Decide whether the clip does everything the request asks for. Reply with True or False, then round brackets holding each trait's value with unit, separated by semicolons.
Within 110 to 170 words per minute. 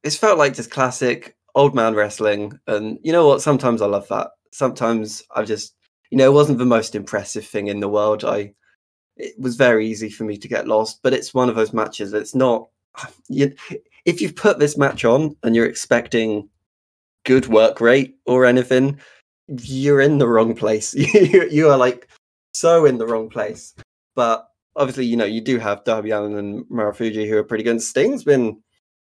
False (195 wpm)